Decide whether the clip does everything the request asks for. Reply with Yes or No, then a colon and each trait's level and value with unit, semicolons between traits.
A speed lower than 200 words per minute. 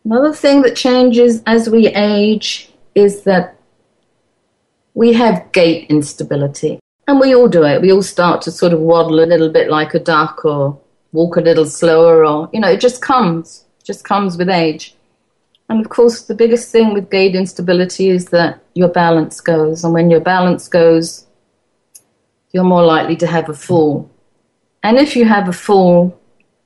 Yes: average, 180 wpm